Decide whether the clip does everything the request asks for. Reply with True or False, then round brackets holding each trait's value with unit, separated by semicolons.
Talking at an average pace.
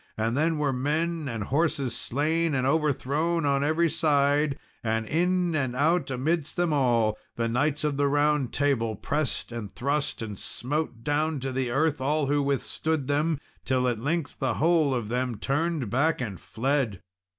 True (170 wpm)